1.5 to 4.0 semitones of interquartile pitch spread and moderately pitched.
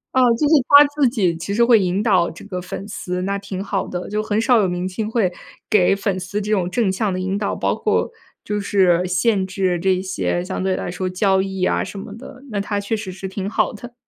No: narrow, 2.5 semitones; high, 195 Hz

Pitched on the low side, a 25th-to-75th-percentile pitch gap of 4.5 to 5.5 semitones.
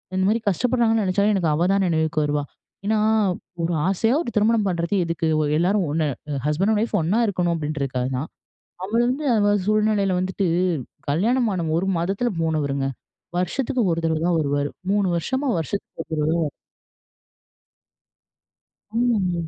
No: medium, 185 Hz; average, 4.8 semitones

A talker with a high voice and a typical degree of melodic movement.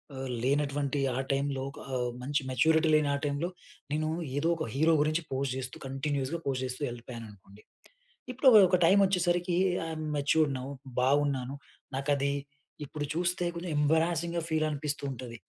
No: medium, 145 Hz; average, 3.4 semitones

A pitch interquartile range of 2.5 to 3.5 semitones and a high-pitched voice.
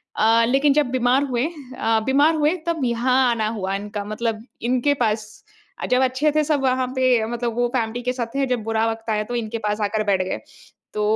Yes: average, 2.9 semitones; high, 240 Hz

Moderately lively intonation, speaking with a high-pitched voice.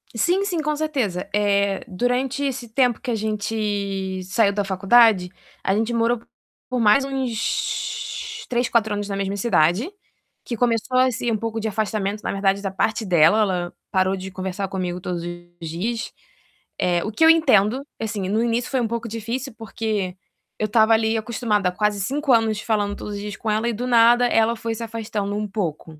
Yes: average, 3.2 semitones; high, 215 Hz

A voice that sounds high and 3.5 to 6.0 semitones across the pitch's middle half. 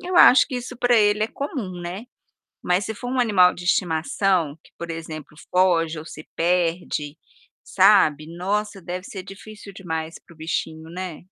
No: medium, 180 Hz; average, 4.1 semitones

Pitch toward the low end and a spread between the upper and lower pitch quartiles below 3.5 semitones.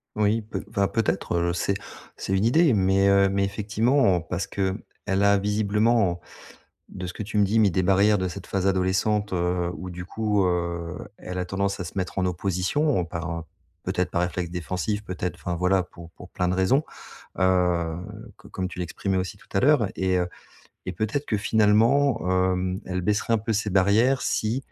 Yes: very low, 95 Hz; narrow, 2.6 semitones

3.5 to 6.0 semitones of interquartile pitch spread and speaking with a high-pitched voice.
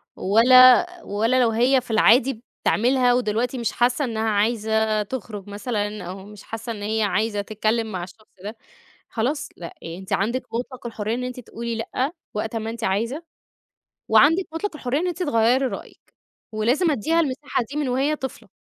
No: average, 3.1 semitones; high, 230 Hz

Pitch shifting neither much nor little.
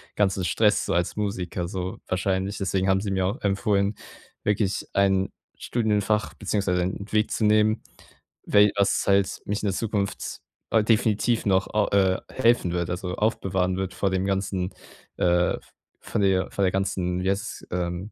No: narrow, 1.9 semitones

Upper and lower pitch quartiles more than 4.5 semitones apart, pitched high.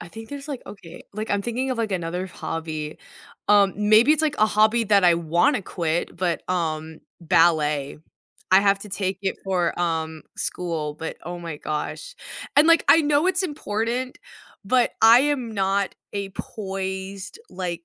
Yes: average, 5.1 semitones; high, 195 Hz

